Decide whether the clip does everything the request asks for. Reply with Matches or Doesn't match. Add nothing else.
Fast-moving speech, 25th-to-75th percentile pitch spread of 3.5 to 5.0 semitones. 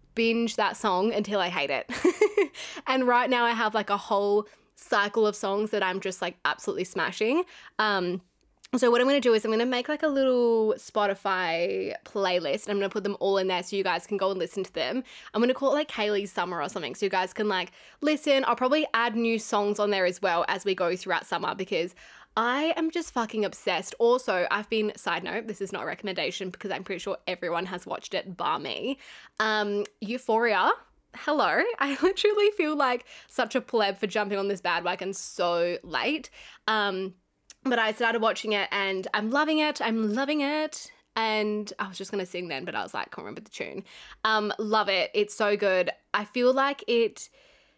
Matches